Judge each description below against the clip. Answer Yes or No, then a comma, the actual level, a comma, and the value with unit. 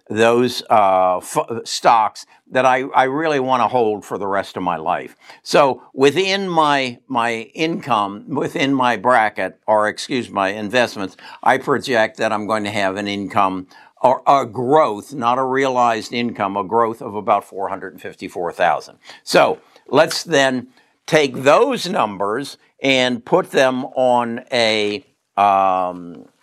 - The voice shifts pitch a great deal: No, average, 4.1 semitones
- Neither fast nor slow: Yes, average, 150 wpm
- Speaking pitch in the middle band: No, low, 120 Hz